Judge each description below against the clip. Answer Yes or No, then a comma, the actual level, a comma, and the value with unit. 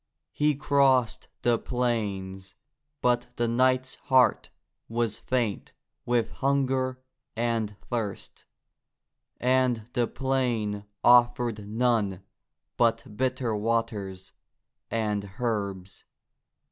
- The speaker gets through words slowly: Yes, slow, 85 wpm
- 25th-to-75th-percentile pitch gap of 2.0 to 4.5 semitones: Yes, average, 3.4 semitones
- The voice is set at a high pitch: No, low, 120 Hz